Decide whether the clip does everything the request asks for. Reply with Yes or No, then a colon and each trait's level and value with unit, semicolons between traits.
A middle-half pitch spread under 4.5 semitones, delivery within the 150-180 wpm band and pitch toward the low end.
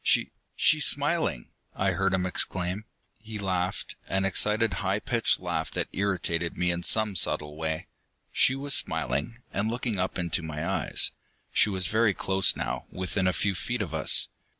Yes: average, 3.5 semitones; average, 170 wpm; very low, 95 Hz